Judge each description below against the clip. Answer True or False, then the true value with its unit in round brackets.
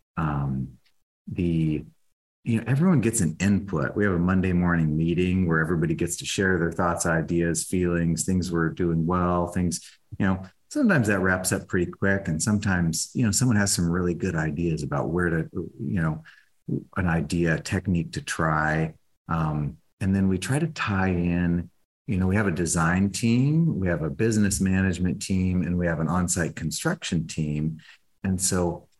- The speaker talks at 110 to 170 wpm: False (180 wpm)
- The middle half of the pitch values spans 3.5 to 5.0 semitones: False (2.8 semitones)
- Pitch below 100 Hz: True (90 Hz)